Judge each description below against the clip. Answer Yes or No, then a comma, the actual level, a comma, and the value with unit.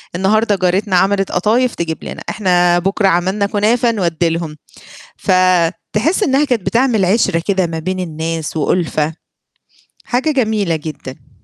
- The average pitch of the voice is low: No, medium, 185 Hz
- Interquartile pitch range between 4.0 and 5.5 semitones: Yes, average, 4.3 semitones